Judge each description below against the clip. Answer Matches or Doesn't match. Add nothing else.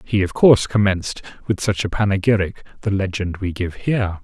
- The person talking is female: Doesn't match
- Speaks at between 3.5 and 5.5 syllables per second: Doesn't match